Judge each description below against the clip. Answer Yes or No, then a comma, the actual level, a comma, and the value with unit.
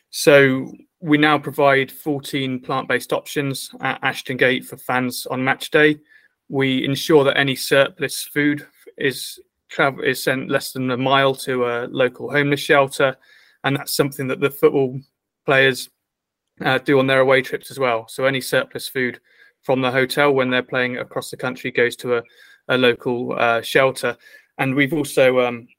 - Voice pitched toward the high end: No, low, 135 Hz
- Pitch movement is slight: Yes, narrow, 2.0 semitones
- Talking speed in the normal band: Yes, average, 170 wpm